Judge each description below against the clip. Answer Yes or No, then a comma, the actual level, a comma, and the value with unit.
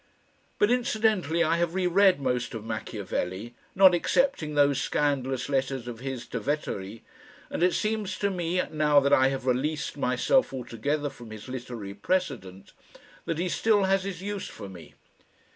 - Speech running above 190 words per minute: No, average, 160 wpm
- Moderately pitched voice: Yes, medium, 145 Hz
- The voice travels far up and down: Yes, wide, 6.9 semitones